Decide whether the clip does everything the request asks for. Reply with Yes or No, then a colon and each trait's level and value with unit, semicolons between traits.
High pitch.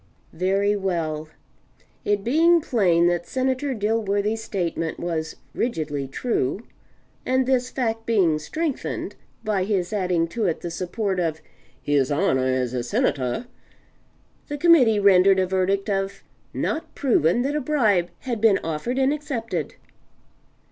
Yes: high, 195 Hz